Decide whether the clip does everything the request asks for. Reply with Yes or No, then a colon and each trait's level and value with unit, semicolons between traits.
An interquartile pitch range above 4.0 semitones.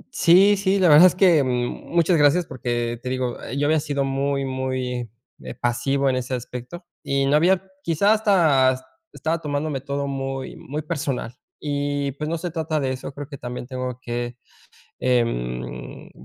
No: average, 3.7 semitones